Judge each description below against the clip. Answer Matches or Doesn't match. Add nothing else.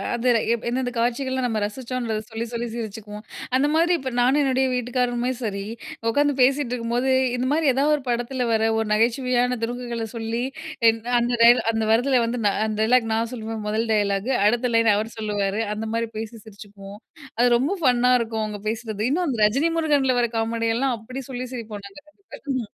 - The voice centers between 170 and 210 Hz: Doesn't match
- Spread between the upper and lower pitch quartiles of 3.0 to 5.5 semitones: Doesn't match